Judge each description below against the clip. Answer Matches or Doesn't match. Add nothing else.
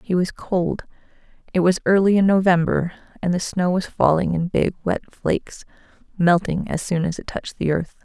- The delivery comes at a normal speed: Matches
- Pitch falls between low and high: Matches